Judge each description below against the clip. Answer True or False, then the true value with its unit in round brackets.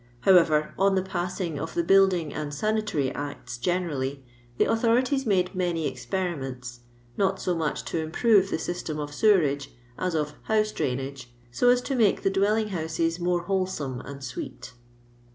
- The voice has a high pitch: False (175 Hz)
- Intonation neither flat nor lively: True (5.0 semitones)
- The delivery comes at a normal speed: True (165 wpm)